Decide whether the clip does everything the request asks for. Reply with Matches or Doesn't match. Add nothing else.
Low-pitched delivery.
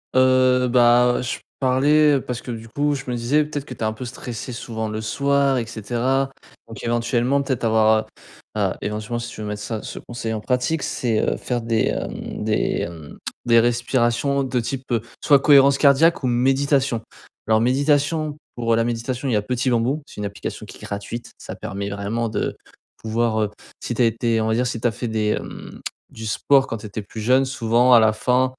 Matches